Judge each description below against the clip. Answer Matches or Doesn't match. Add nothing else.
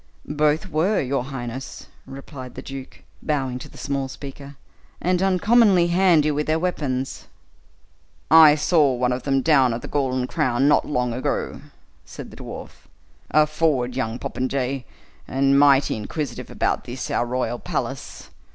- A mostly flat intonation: Doesn't match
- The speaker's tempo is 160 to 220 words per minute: Doesn't match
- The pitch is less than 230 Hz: Matches